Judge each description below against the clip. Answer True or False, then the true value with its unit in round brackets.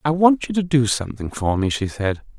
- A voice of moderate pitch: False (125 Hz)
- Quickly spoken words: True (250 wpm)